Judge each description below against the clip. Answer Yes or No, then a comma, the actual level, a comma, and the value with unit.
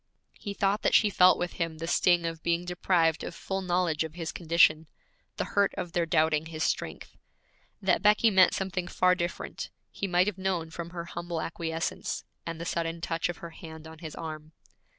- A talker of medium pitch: Yes, medium, 170 Hz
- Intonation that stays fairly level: Yes, narrow, 2.0 semitones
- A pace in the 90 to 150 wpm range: No, average, 195 wpm